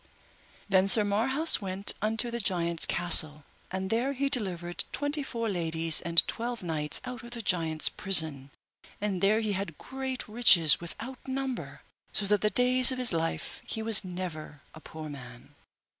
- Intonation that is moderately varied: No, wide, 6.1 semitones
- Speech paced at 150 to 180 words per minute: Yes, average, 160 wpm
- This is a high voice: Yes, high, 195 Hz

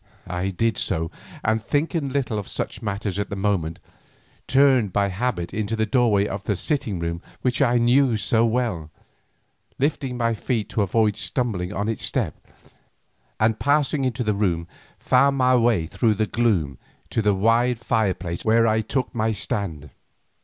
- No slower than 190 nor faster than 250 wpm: No, average, 165 wpm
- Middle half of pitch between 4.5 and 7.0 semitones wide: No, average, 3.8 semitones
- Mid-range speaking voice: No, low, 110 Hz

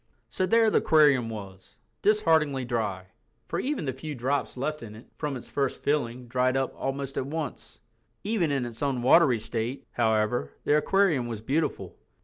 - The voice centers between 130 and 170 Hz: Yes, low, 135 Hz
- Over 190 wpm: No, average, 160 wpm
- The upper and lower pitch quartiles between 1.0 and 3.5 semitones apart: No, average, 4.4 semitones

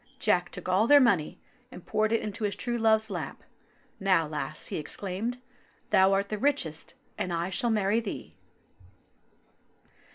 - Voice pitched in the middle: No, high, 200 Hz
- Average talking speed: Yes, average, 155 wpm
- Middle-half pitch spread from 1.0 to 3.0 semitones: No, average, 3.7 semitones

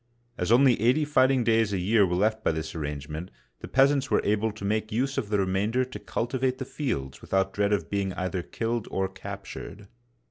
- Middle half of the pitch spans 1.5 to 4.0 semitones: No, average, 4.6 semitones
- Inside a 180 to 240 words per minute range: Yes, fast, 205 wpm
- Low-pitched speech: Yes, low, 105 Hz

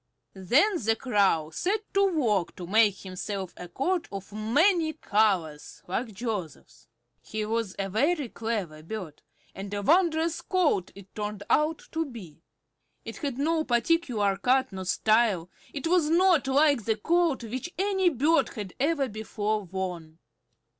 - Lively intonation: Yes, wide, 8.2 semitones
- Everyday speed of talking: Yes, average, 145 wpm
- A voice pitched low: No, high, 225 Hz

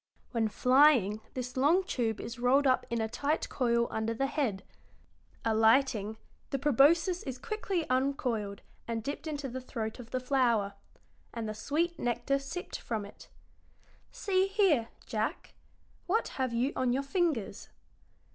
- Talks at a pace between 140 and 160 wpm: Yes, average, 145 wpm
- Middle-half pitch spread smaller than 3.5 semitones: No, average, 4.2 semitones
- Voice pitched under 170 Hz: No, very high, 255 Hz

